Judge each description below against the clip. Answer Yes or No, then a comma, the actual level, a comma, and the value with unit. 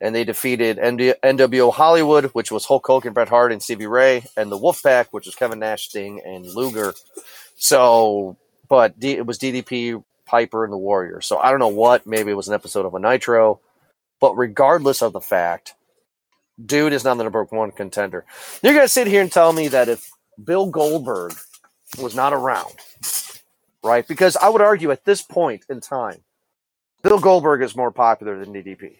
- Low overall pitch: Yes, low, 120 Hz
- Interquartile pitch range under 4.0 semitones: No, average, 4.3 semitones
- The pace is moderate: Yes, average, 190 wpm